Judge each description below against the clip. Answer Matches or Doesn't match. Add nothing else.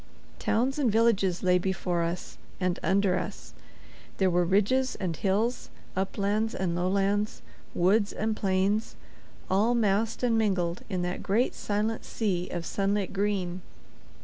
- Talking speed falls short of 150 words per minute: Matches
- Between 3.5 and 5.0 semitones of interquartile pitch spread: Doesn't match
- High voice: Matches